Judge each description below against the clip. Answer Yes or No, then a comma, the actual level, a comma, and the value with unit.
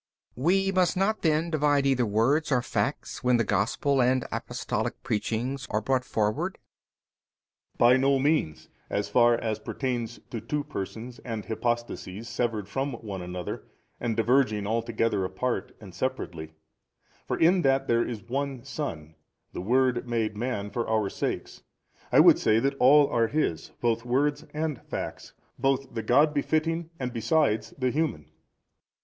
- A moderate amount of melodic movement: Yes, average, 4.1 semitones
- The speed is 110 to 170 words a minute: Yes, average, 155 wpm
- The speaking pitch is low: Yes, low, 120 Hz